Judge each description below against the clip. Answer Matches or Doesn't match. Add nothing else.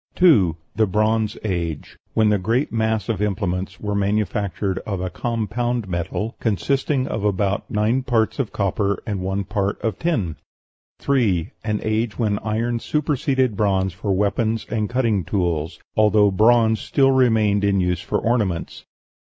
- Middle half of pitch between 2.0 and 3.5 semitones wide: Matches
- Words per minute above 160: Doesn't match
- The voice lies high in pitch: Doesn't match